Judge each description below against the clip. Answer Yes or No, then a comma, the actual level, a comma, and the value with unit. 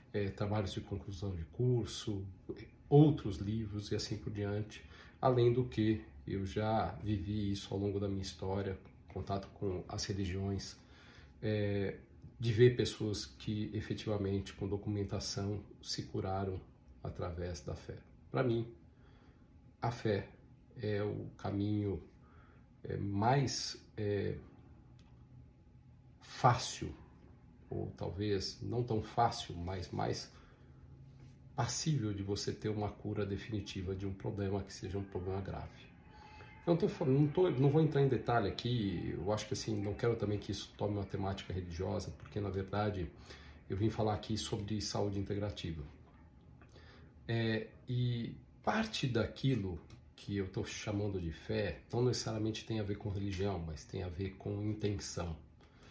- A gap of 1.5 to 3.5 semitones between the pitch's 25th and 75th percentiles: Yes, narrow, 2.4 semitones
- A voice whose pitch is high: No, low, 105 Hz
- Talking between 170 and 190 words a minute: No, average, 140 wpm